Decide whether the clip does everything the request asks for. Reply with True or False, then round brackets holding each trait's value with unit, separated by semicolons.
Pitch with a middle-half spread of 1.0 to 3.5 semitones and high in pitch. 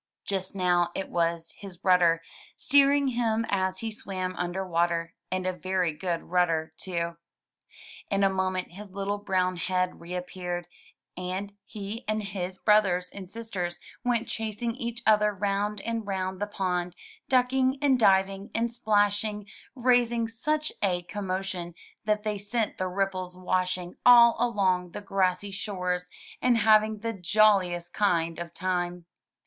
True (3.1 semitones; 195 Hz)